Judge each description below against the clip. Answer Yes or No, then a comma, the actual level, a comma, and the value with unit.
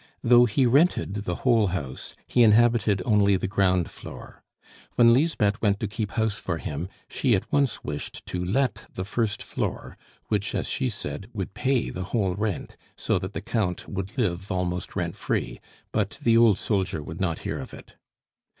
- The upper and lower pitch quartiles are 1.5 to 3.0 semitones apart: No, average, 4.1 semitones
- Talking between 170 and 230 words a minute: Yes, average, 180 wpm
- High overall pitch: No, low, 100 Hz